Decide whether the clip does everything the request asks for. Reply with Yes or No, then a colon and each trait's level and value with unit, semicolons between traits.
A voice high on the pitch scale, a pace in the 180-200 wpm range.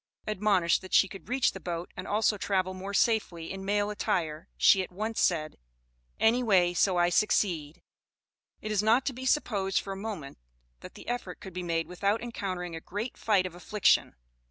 Yes: high, 195 Hz; average, 190 wpm